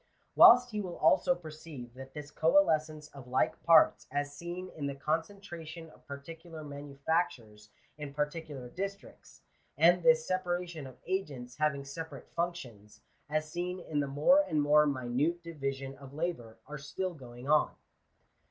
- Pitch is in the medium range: Yes, medium, 155 Hz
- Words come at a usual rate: Yes, average, 150 wpm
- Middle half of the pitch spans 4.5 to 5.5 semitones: No, average, 3.7 semitones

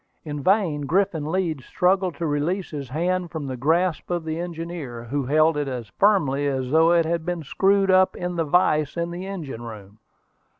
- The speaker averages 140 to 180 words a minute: No, average, 195 wpm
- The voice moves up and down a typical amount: Yes, average, 3.7 semitones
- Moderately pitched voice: Yes, medium, 160 Hz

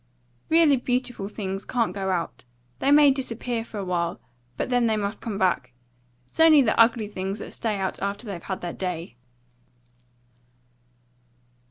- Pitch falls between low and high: No, high, 210 Hz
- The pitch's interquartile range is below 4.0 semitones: No, average, 4.5 semitones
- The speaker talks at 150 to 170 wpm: Yes, average, 160 wpm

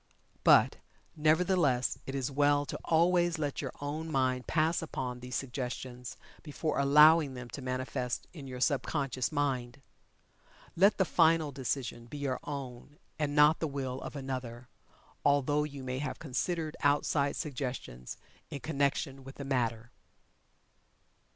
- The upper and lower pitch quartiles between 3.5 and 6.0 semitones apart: No, average, 2.9 semitones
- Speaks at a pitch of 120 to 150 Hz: Yes, medium, 140 Hz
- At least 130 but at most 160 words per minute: Yes, average, 140 wpm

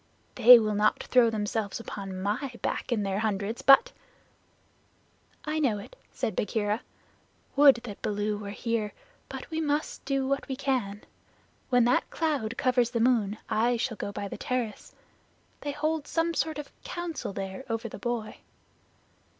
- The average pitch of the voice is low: No, high, 235 Hz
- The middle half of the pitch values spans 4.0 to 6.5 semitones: Yes, average, 4.7 semitones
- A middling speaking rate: Yes, average, 160 wpm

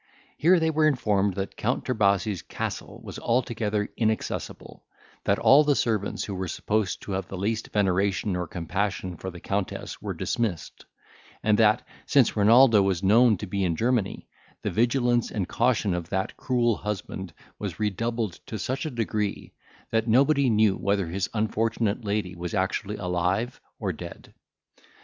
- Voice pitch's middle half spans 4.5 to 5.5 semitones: No, average, 3.5 semitones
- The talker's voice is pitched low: Yes, low, 105 Hz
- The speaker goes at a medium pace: Yes, average, 160 wpm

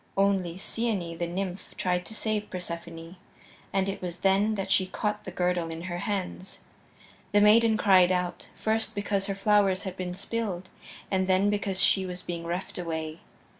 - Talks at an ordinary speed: Yes, average, 170 wpm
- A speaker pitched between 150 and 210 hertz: Yes, high, 190 Hz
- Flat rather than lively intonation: Yes, narrow, 2.3 semitones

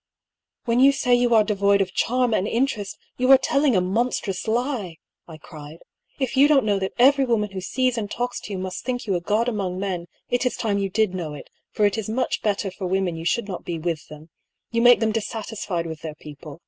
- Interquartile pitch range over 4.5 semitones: Yes, average, 5.0 semitones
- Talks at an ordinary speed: No, fast, 240 wpm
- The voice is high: Yes, high, 210 Hz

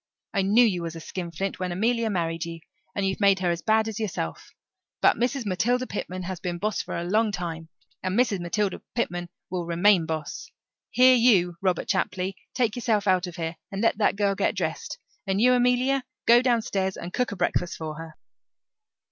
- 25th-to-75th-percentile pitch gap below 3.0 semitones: No, average, 4.2 semitones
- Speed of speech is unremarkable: Yes, average, 195 wpm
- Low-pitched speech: No, high, 195 Hz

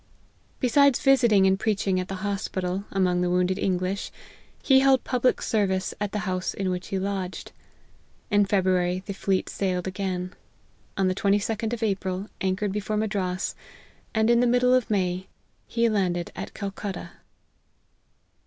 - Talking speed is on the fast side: No, average, 155 wpm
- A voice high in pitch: Yes, high, 195 Hz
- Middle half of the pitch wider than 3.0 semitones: No, narrow, 2.5 semitones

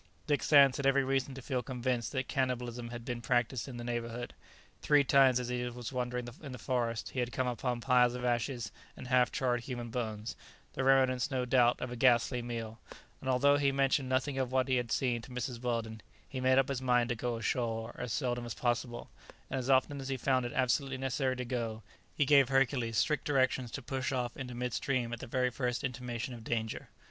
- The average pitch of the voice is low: Yes, low, 125 Hz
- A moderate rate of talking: No, fast, 220 wpm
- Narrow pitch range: Yes, narrow, 1.7 semitones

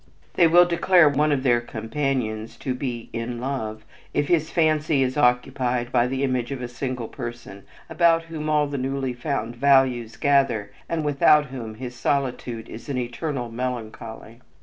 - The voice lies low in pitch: Yes, low, 130 Hz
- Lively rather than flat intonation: No, average, 3.4 semitones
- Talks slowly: No, average, 165 wpm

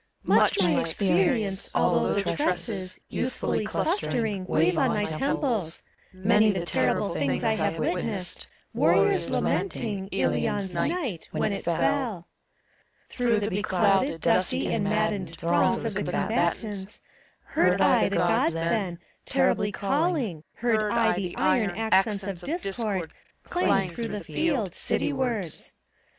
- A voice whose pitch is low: No, high, 200 Hz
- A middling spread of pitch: Yes, average, 3.9 semitones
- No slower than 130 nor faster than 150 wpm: Yes, slow, 135 wpm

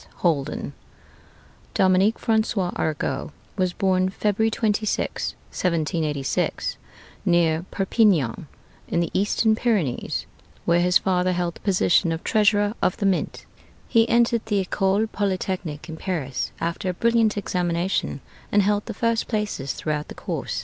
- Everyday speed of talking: No, slow, 130 wpm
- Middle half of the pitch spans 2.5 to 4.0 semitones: Yes, average, 3.7 semitones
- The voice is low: No, medium, 185 Hz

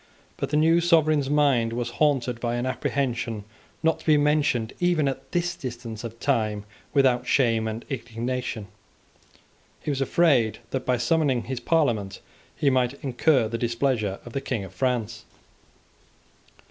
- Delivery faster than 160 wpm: No, average, 150 wpm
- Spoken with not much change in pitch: No, average, 4.0 semitones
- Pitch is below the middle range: Yes, low, 125 Hz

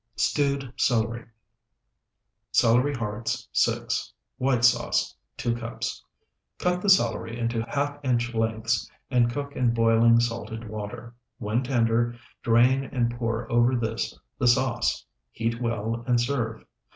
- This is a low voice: Yes, low, 120 Hz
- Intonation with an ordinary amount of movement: No, narrow, 1.6 semitones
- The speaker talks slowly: Yes, slow, 125 wpm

